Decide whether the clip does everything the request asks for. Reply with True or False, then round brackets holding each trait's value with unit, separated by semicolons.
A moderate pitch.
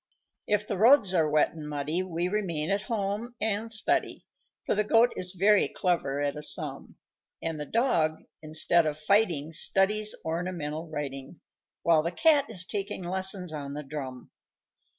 True (175 Hz)